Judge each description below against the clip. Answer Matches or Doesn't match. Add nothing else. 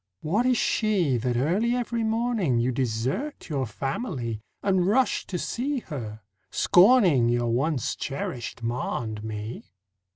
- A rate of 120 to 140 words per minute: Matches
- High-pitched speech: Doesn't match